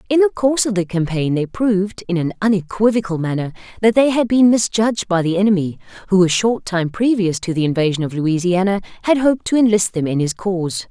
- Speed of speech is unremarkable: No, fast, 210 wpm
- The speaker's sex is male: No, female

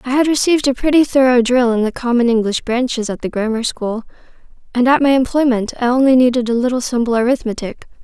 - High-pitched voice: Yes, high, 245 Hz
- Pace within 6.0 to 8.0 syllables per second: Yes, 6.2 syllables/s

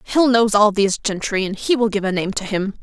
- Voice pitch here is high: Yes, high, 210 Hz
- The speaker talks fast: Yes, fast, 275 wpm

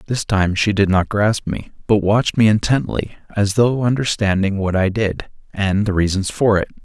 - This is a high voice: No, low, 105 Hz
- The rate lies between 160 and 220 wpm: Yes, average, 195 wpm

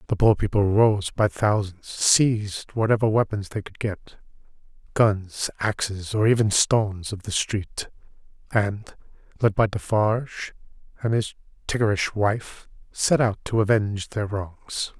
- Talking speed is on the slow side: Yes, slow, 130 wpm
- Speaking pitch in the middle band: No, low, 105 Hz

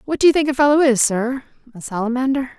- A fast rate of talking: Yes, fast, 210 wpm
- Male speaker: No, female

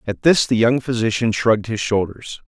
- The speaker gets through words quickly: No, average, 190 wpm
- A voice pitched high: No, low, 115 Hz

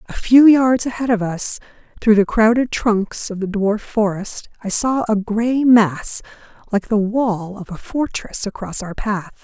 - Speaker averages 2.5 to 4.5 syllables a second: Yes, 4.1 syllables/s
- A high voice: Yes, high, 215 Hz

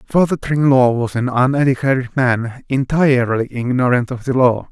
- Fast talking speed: No, average, 140 wpm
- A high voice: No, low, 130 Hz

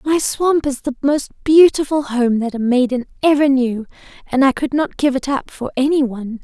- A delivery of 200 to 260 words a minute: Yes, fast, 205 wpm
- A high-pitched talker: Yes, very high, 270 Hz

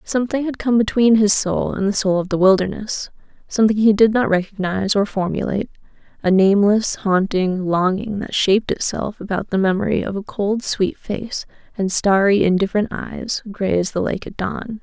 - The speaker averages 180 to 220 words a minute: No, average, 170 wpm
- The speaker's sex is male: No, female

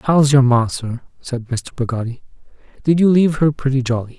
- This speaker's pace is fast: No, average, 185 wpm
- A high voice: No, low, 135 Hz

